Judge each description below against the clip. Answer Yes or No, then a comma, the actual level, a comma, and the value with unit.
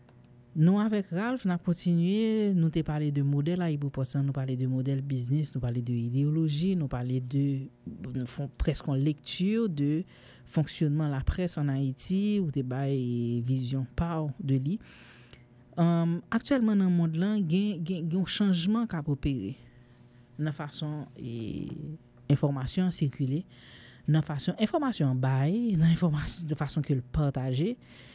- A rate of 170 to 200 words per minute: No, average, 140 wpm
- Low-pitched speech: No, medium, 150 Hz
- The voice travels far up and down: No, average, 4.9 semitones